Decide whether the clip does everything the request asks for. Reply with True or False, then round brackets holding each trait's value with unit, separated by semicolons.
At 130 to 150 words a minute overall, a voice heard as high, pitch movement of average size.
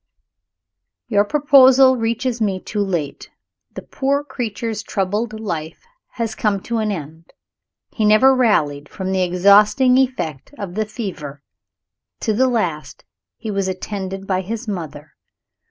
True (135 wpm; 210 Hz; 4.2 semitones)